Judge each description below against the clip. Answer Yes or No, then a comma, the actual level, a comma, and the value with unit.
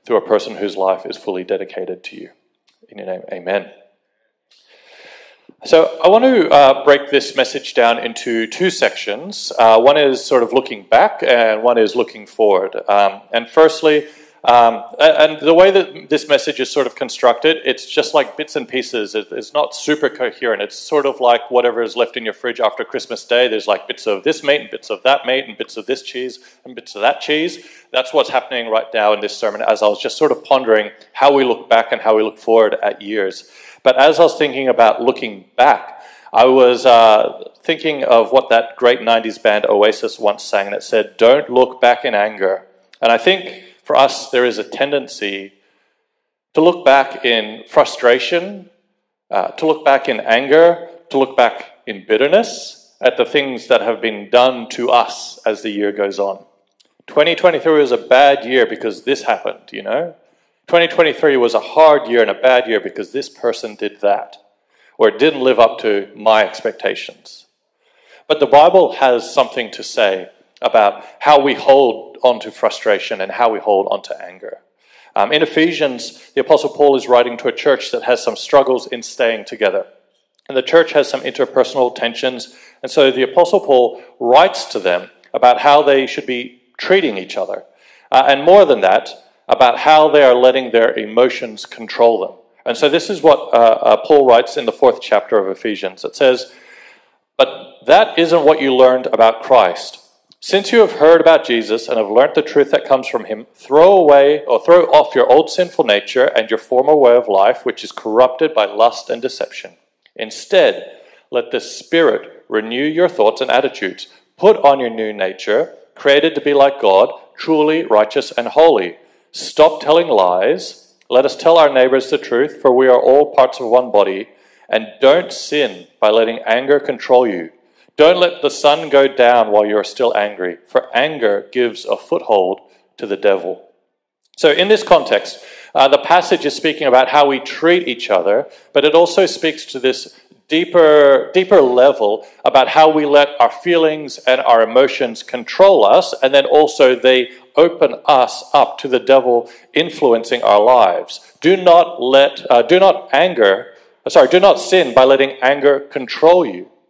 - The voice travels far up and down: Yes, wide, 6.5 semitones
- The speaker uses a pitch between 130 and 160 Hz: Yes, medium, 140 Hz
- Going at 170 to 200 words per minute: Yes, average, 190 wpm